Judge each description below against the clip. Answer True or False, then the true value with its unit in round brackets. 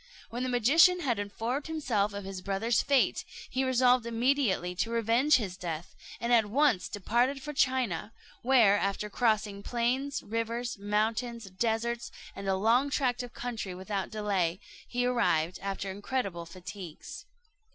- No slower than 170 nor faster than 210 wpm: False (145 wpm)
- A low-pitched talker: False (230 Hz)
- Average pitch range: True (4.0 semitones)